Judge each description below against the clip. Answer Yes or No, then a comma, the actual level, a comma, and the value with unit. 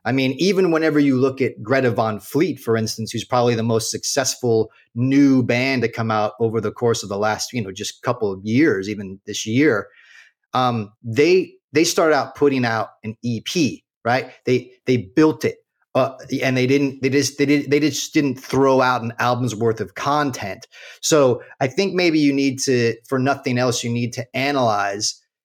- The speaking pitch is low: Yes, low, 125 Hz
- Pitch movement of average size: Yes, average, 3.6 semitones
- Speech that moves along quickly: No, average, 195 wpm